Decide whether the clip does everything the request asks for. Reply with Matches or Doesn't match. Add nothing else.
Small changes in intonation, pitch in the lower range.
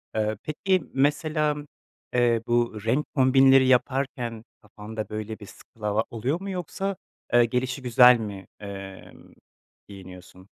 Doesn't match